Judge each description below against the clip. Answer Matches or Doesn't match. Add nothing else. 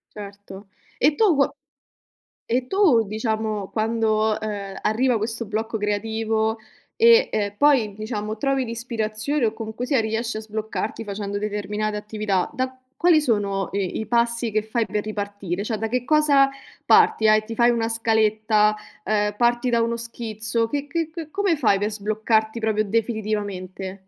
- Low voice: Doesn't match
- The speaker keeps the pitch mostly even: Matches